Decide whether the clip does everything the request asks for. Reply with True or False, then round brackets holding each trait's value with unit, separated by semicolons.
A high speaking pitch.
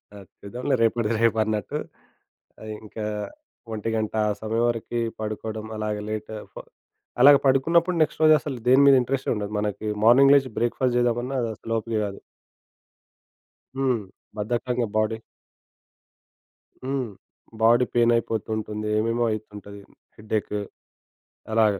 False (115 Hz)